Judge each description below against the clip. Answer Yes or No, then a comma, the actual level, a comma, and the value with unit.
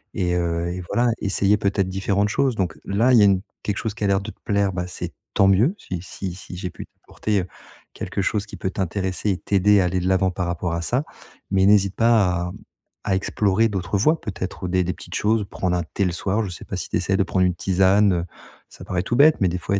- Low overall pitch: Yes, very low, 95 Hz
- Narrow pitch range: Yes, narrow, 2.2 semitones